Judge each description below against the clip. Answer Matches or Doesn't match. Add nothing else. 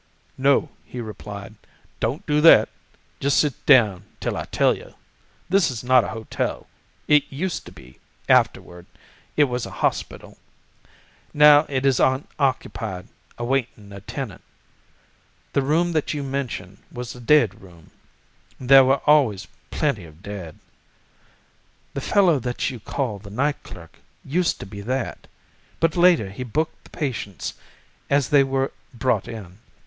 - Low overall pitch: Matches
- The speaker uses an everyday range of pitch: Doesn't match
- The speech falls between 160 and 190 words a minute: Doesn't match